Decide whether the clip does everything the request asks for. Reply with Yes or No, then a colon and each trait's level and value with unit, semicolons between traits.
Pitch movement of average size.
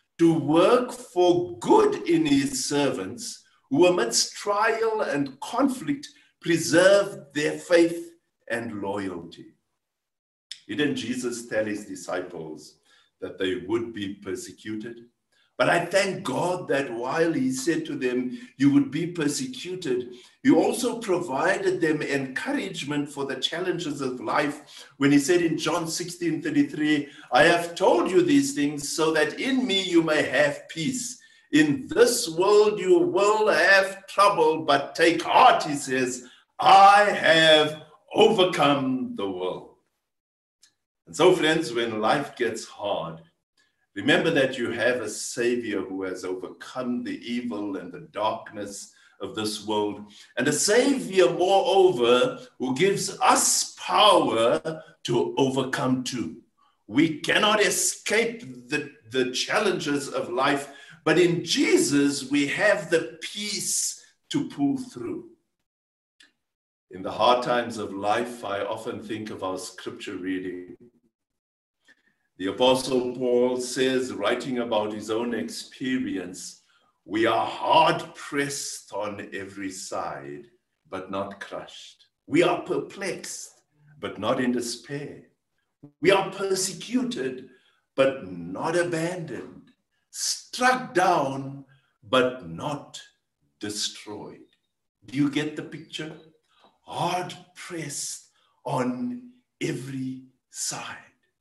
No: wide, 8.2 semitones